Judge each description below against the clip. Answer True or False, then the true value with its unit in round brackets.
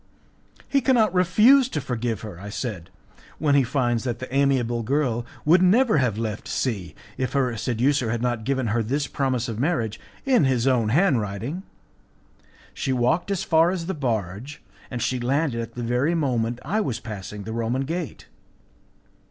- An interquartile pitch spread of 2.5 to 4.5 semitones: False (4.9 semitones)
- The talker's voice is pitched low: True (125 Hz)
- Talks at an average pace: True (170 wpm)